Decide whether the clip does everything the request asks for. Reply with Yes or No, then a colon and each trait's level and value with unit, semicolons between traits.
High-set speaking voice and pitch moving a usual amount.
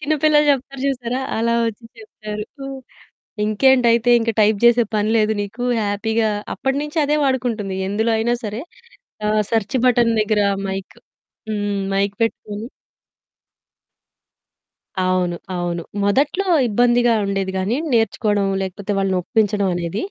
Yes: high, 220 Hz; average, 3.2 semitones